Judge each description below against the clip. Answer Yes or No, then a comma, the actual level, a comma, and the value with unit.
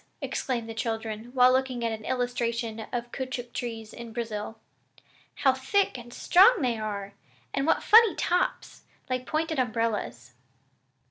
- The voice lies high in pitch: Yes, high, 240 Hz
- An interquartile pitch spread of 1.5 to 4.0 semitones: Yes, average, 2.7 semitones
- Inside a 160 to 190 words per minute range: No, average, 140 wpm